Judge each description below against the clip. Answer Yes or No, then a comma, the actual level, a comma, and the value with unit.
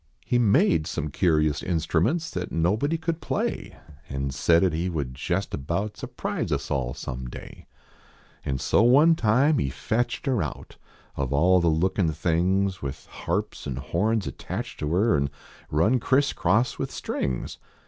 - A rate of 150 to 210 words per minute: Yes, average, 160 wpm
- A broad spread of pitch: Yes, wide, 7.2 semitones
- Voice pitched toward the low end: Yes, very low, 90 Hz